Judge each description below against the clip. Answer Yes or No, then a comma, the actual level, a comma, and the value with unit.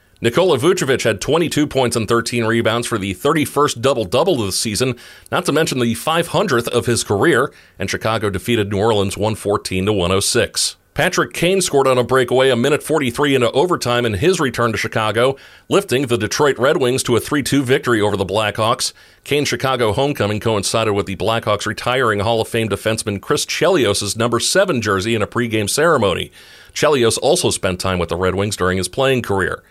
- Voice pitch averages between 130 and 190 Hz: No, low, 115 Hz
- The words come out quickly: No, average, 190 wpm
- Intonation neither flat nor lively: Yes, average, 4.0 semitones